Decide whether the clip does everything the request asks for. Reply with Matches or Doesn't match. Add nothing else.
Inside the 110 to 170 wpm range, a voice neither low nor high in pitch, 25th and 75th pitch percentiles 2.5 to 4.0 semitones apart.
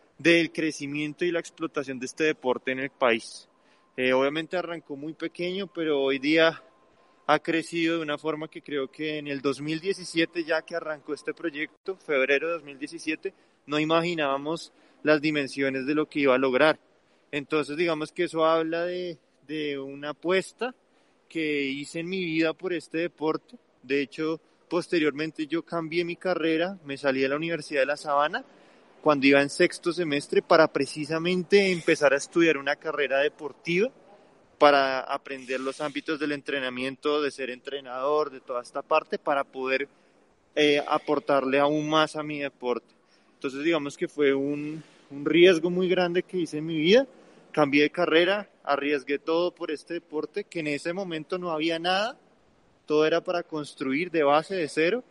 Matches